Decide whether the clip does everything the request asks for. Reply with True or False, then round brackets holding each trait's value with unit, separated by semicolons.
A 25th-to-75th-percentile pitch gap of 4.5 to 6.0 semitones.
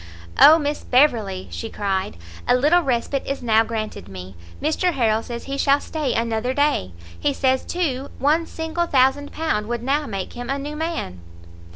True (4.9 semitones)